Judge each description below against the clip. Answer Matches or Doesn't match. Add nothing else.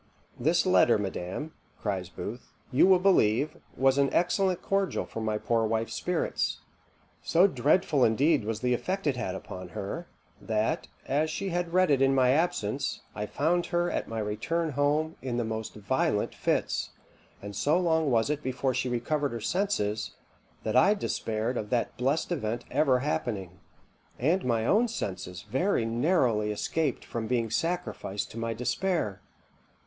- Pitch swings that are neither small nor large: Doesn't match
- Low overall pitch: Matches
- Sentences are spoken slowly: Doesn't match